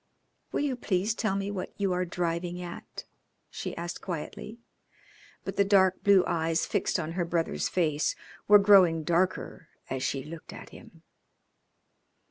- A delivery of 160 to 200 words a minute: No, average, 150 wpm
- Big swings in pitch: No, average, 2.9 semitones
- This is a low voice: No, medium, 180 Hz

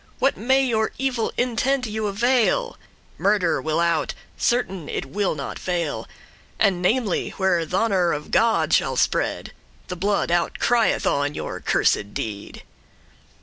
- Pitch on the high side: Yes, high, 200 Hz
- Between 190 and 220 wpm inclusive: No, average, 145 wpm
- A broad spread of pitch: Yes, wide, 5.9 semitones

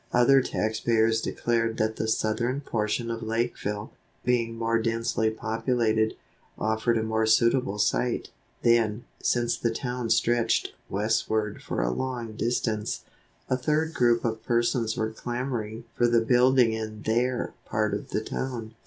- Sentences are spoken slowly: No, average, 145 wpm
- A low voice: Yes, low, 115 Hz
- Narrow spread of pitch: Yes, narrow, 1.6 semitones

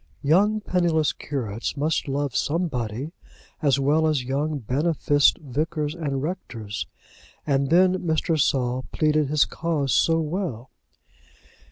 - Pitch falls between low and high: Yes, medium, 150 Hz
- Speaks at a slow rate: Yes, slow, 120 wpm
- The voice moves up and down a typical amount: Yes, average, 3.3 semitones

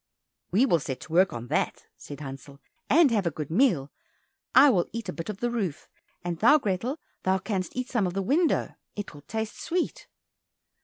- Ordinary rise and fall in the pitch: No, wide, 6.9 semitones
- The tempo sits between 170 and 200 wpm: Yes, average, 195 wpm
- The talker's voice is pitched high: Yes, high, 195 Hz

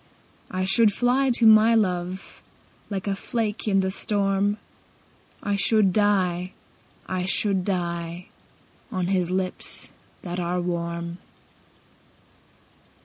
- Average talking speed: No, slow, 110 wpm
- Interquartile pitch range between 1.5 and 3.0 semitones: Yes, narrow, 2.5 semitones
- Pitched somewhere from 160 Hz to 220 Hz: Yes, high, 190 Hz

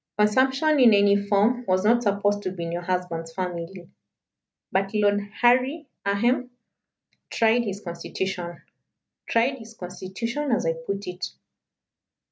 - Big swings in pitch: No, average, 4.5 semitones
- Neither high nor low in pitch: No, high, 200 Hz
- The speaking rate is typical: No, slow, 130 wpm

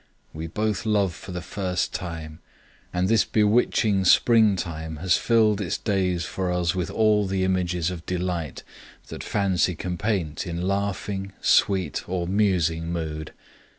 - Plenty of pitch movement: No, average, 2.9 semitones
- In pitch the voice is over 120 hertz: No, very low, 90 Hz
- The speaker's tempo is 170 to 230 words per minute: No, average, 145 wpm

